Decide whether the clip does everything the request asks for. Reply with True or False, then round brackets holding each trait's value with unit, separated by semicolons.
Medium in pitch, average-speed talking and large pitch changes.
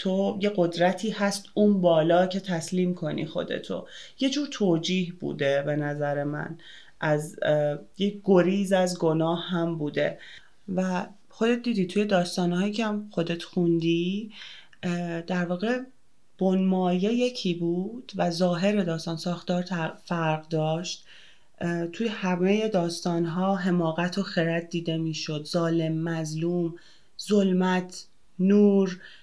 False (180 Hz; 115 wpm; 2.9 semitones)